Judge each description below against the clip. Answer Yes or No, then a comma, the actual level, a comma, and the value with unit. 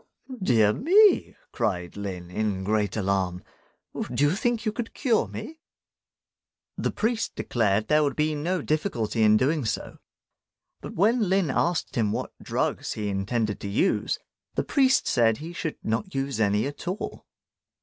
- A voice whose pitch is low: Yes, low, 130 Hz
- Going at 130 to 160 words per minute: Yes, average, 155 wpm